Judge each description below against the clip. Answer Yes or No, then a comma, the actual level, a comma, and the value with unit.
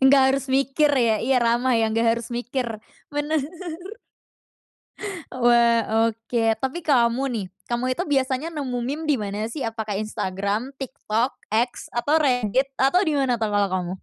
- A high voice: Yes, high, 240 Hz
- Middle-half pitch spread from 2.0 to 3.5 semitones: Yes, average, 3.1 semitones